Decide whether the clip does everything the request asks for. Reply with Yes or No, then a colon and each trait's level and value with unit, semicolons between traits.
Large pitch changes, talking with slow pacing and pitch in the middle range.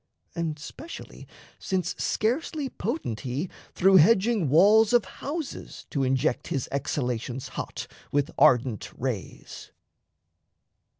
Yes: wide, 9.0 semitones; slow, 105 wpm; medium, 165 Hz